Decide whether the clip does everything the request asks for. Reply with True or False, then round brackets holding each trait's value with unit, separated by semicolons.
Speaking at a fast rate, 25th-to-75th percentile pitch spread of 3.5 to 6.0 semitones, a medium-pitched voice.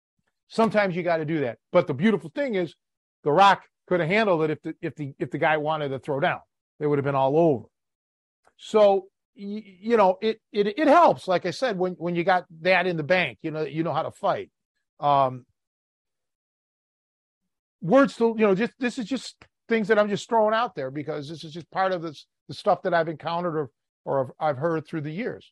True (225 wpm; 4.9 semitones; 175 Hz)